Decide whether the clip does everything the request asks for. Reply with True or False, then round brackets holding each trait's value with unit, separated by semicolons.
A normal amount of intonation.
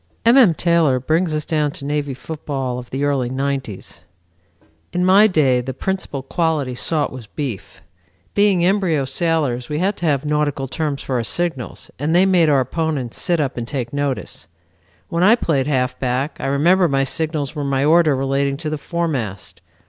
True (3.9 semitones)